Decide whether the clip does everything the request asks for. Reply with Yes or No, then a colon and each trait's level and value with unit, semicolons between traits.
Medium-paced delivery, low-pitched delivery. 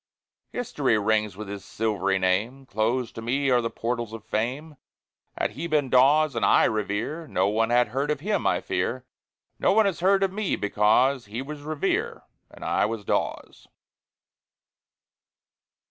Yes: average, 160 wpm; low, 120 Hz